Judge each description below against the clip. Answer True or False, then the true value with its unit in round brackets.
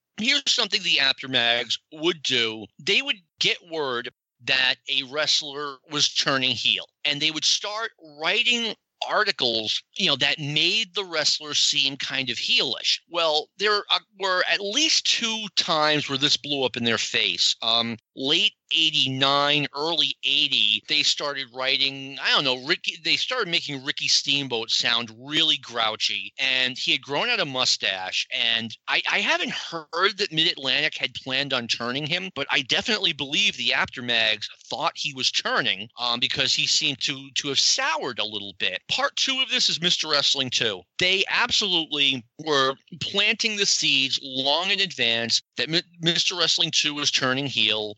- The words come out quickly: False (165 wpm)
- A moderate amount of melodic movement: True (4.7 semitones)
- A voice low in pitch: False (145 Hz)